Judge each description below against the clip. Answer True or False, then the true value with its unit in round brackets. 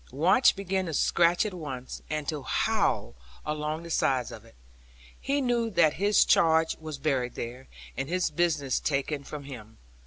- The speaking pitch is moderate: True (155 Hz)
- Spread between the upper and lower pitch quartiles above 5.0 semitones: False (4.3 semitones)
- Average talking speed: True (165 wpm)